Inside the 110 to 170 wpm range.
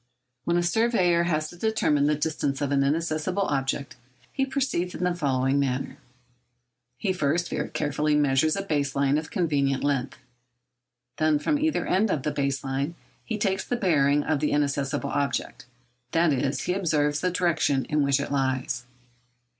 Yes: average, 165 wpm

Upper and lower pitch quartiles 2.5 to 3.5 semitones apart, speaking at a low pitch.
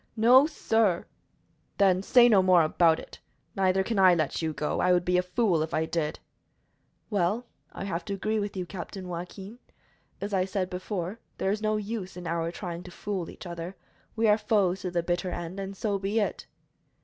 No: average, 2.9 semitones; medium, 185 Hz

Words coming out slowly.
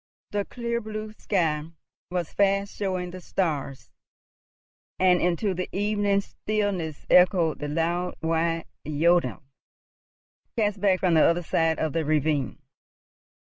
Yes: slow, 125 wpm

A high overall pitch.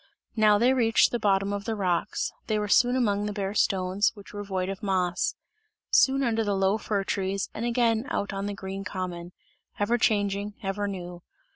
Yes: high, 205 Hz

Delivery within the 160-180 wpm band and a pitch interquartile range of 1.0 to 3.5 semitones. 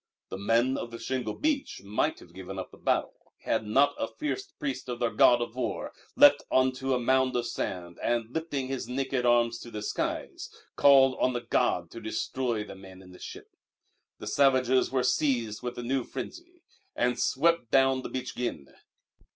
No: average, 190 wpm; average, 2.7 semitones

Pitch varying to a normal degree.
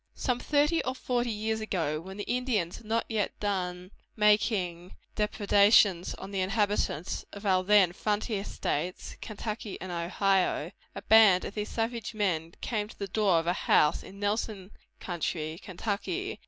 Yes: average, 3.3 semitones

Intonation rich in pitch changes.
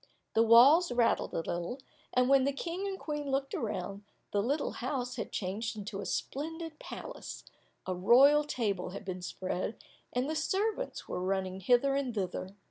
Yes: wide, 6.7 semitones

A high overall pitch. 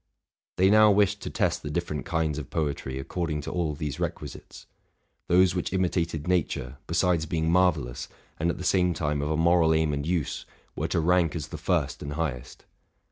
No: very low, 80 Hz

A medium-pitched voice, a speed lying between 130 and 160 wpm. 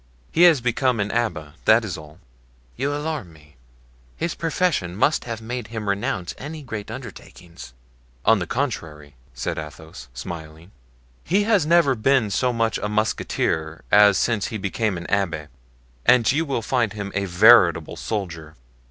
No: low, 105 Hz; average, 155 wpm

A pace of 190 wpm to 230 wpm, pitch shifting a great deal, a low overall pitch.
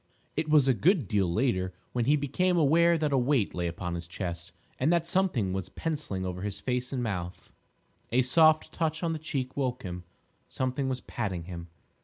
Yes: average, 195 wpm; wide, 8.6 semitones; low, 125 Hz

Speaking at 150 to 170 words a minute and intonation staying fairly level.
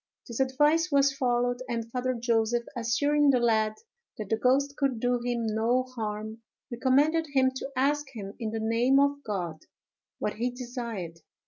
No: average, 160 wpm; average, 3.2 semitones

